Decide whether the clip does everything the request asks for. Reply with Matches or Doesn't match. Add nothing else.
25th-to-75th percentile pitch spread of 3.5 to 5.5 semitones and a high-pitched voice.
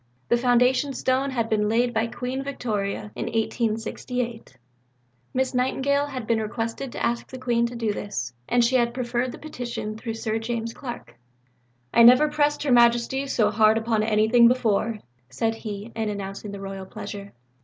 Doesn't match